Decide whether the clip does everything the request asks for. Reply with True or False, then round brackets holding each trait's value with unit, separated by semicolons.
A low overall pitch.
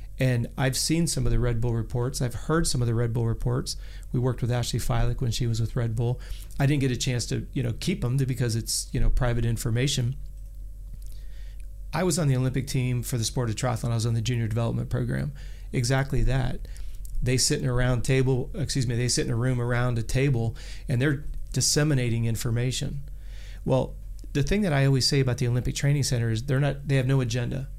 True (125 Hz)